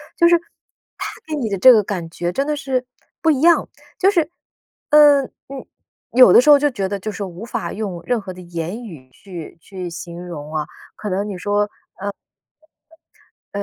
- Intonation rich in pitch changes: Yes, wide, 7.5 semitones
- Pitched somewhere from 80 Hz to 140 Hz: No, high, 205 Hz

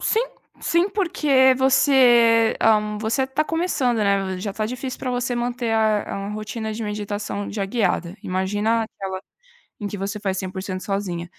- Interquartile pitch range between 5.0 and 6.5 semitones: No, average, 3.8 semitones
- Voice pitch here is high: Yes, high, 215 Hz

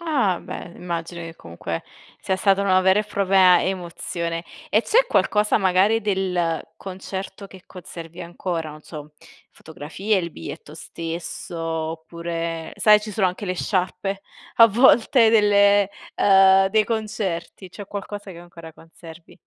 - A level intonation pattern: No, average, 3.3 semitones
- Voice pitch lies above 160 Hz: Yes, medium, 185 Hz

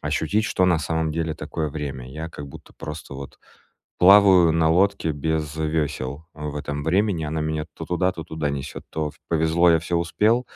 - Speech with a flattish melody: Yes, narrow, 2.3 semitones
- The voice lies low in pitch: Yes, very low, 80 Hz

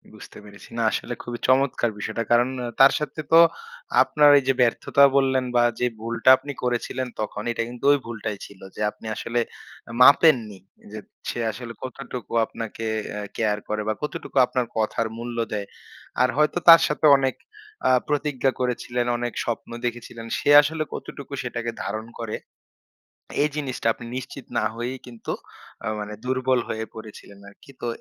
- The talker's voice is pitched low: Yes, low, 120 Hz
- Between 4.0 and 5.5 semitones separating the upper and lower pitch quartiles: No, average, 2.8 semitones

